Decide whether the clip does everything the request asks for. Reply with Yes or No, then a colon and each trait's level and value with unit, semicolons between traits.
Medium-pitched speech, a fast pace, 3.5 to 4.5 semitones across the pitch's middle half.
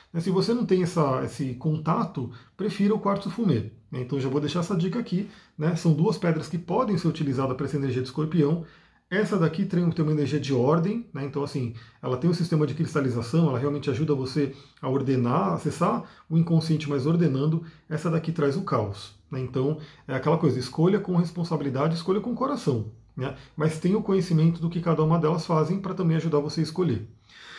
Yes: medium, 155 Hz; fast, 200 wpm; average, 3.8 semitones